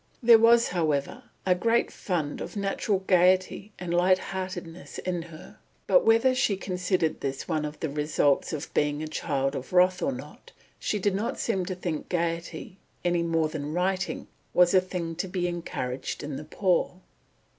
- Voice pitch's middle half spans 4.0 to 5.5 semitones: No, average, 3.2 semitones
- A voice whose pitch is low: No, medium, 180 Hz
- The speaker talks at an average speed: Yes, average, 175 wpm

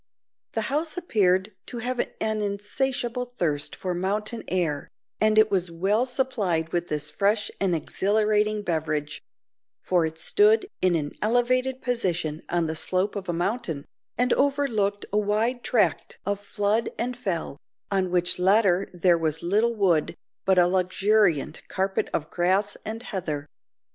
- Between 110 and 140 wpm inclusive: No, average, 150 wpm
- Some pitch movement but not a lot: Yes, average, 4.5 semitones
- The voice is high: Yes, high, 200 Hz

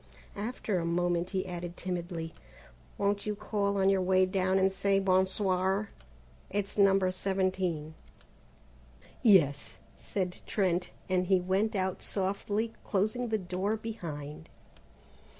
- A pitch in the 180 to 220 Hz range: Yes, high, 190 Hz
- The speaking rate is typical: No, slow, 125 wpm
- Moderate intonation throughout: No, narrow, 2.0 semitones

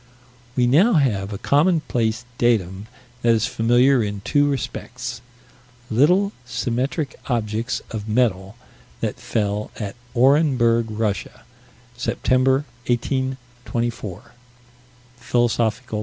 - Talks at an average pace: No, slow, 95 wpm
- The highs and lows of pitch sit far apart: No, average, 3.2 semitones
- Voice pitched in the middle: No, low, 120 Hz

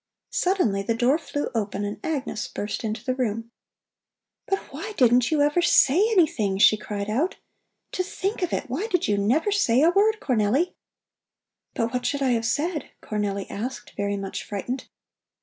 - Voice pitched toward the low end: No, very high, 250 Hz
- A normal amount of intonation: No, wide, 7.8 semitones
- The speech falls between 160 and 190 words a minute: Yes, average, 170 wpm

